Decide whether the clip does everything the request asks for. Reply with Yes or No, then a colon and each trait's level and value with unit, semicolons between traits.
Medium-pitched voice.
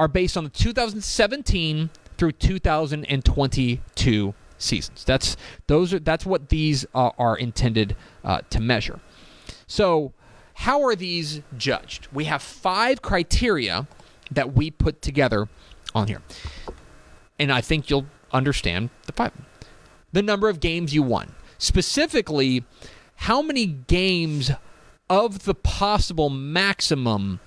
Yes: medium, 150 Hz